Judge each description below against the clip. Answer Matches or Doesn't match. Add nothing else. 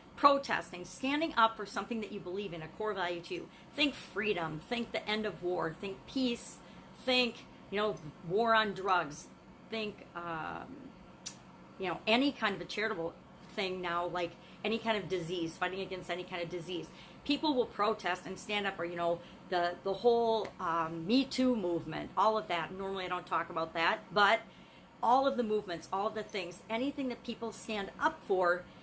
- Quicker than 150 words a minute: Matches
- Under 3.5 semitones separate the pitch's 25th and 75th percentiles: Doesn't match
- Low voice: Doesn't match